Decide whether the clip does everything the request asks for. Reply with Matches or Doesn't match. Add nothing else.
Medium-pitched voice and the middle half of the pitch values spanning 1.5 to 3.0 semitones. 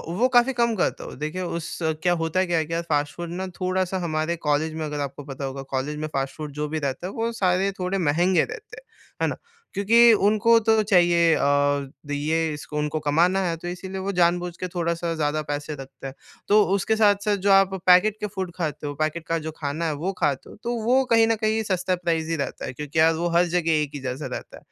Doesn't match